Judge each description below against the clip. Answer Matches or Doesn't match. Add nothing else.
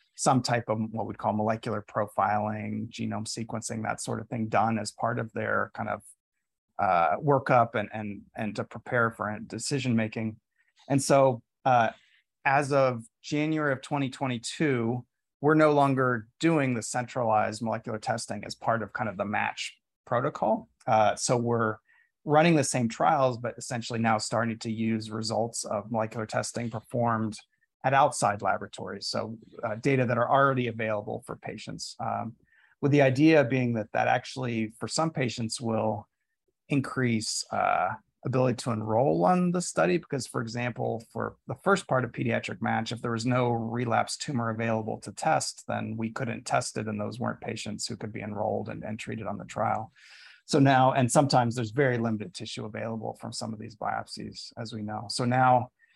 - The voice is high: Doesn't match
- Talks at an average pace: Matches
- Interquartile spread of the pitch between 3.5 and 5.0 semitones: Doesn't match